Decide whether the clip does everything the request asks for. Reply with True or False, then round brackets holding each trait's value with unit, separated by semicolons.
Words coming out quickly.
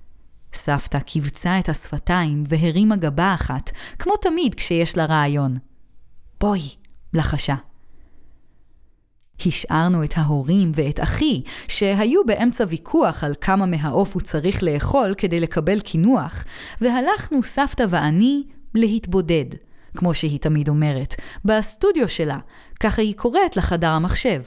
False (115 wpm)